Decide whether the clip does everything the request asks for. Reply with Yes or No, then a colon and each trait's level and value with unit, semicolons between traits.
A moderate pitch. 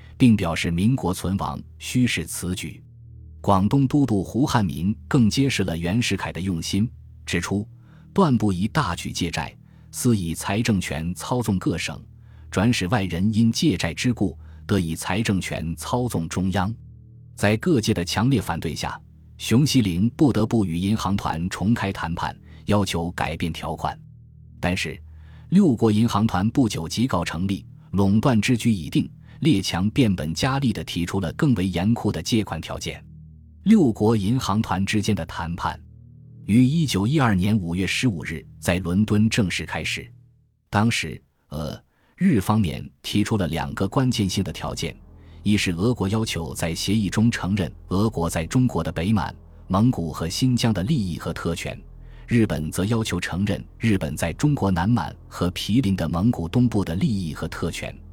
No: low, 100 Hz